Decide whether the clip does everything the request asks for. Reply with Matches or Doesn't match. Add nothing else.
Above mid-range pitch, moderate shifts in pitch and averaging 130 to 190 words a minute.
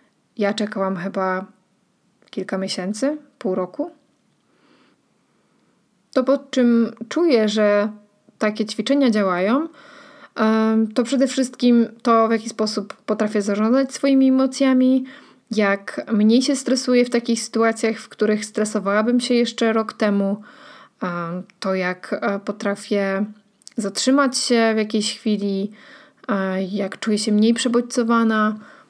Doesn't match